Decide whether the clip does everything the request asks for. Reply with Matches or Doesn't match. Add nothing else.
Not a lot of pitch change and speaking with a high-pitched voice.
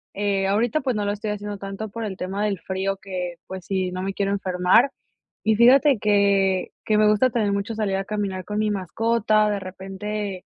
Matches